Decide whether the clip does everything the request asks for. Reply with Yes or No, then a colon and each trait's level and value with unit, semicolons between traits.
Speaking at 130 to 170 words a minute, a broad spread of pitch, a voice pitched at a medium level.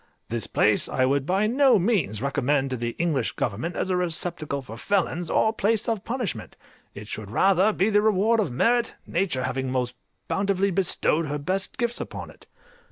No: average, 180 wpm; wide, 7.8 semitones; medium, 175 Hz